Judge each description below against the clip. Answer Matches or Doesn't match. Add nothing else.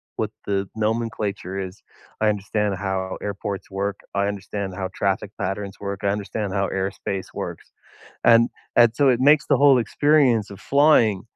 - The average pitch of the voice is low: Matches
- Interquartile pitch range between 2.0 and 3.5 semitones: Matches